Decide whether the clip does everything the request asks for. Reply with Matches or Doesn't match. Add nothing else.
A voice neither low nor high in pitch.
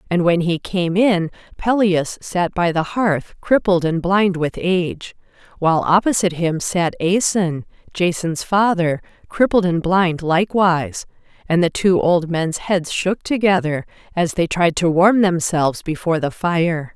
Matches